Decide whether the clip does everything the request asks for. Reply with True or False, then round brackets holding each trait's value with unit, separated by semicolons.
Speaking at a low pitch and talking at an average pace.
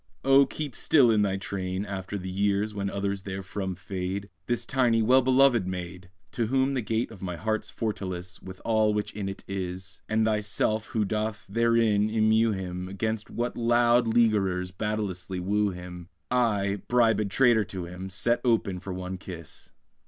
True (105 Hz; 175 wpm)